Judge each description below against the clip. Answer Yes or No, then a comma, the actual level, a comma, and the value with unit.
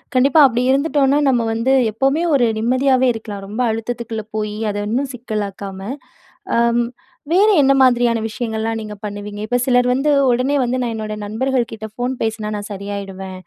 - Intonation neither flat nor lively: Yes, average, 3.4 semitones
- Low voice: No, high, 235 Hz